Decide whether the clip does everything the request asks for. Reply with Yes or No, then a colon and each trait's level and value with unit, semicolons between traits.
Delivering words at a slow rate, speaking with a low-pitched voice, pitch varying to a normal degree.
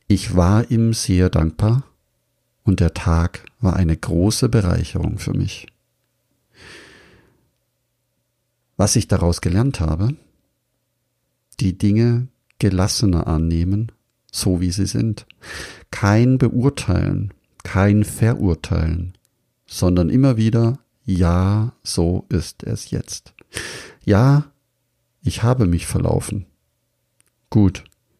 Yes: slow, 95 wpm; low, 105 Hz; average, 4.6 semitones